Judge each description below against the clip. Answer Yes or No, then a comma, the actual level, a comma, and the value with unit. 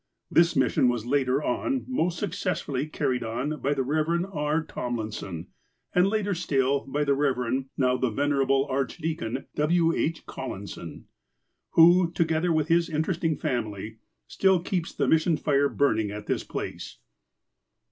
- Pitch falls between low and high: Yes, medium, 145 Hz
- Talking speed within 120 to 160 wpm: Yes, average, 145 wpm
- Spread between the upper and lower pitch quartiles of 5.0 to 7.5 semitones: No, average, 4.5 semitones